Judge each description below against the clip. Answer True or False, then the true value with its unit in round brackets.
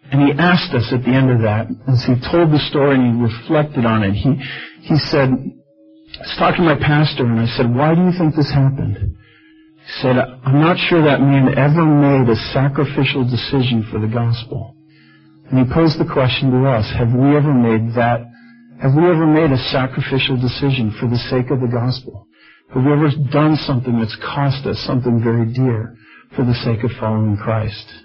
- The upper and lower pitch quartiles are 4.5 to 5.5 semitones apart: False (3.8 semitones)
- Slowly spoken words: False (200 wpm)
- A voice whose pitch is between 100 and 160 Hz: True (130 Hz)